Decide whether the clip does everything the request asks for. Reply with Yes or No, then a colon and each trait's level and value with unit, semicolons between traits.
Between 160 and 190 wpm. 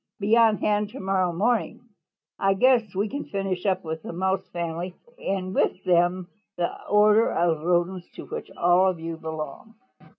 Yes: average, 175 wpm